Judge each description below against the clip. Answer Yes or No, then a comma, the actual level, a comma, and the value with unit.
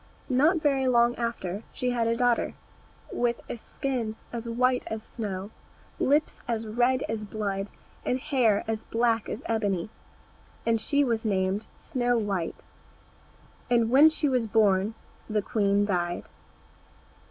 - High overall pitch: Yes, high, 230 Hz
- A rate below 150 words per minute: Yes, average, 140 wpm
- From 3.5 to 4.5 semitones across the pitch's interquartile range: No, average, 3.0 semitones